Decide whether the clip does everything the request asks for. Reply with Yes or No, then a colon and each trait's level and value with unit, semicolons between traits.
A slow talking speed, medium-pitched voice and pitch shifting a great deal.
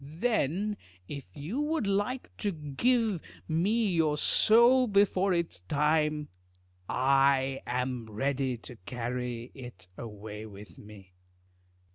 Yes: slow, 110 wpm; medium, 145 Hz; wide, 8.3 semitones